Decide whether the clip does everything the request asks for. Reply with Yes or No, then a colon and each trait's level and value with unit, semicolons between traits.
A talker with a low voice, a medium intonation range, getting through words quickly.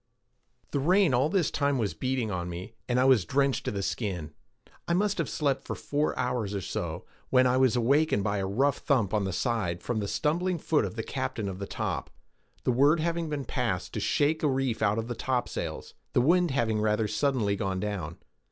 No: low, 125 Hz; wide, 5.7 semitones; fast, 215 wpm